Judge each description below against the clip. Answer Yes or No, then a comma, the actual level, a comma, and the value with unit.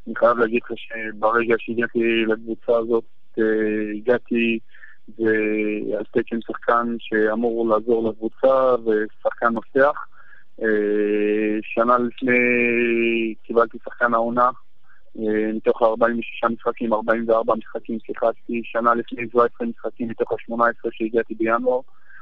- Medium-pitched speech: No, low, 115 Hz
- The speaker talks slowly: Yes, slow, 95 wpm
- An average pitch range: No, narrow, 1.2 semitones